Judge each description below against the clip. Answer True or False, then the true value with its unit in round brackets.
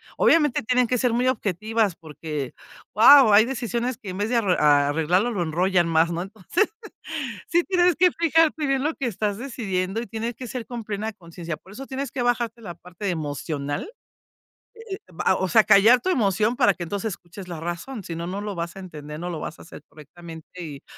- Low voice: False (205 Hz)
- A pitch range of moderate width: False (6.1 semitones)